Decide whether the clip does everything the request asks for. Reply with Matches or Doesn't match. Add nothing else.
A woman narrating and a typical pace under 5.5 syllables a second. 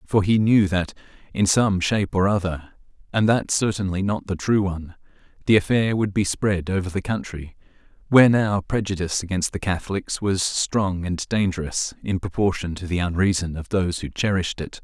Doesn't match